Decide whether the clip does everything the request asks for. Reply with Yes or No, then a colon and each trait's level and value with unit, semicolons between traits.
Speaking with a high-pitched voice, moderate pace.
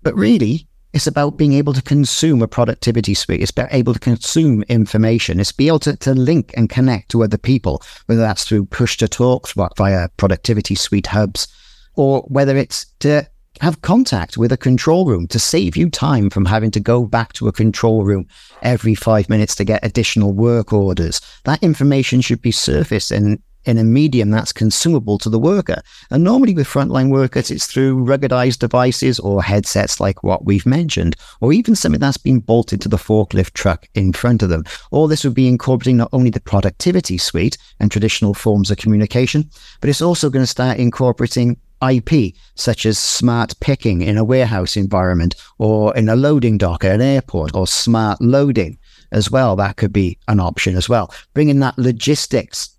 No: low, 115 Hz; average, 190 wpm